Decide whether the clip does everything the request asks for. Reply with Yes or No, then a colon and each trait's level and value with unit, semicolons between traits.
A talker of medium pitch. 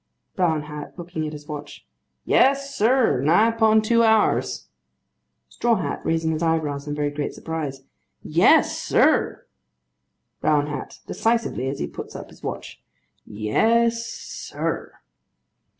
Yes: medium, 160 Hz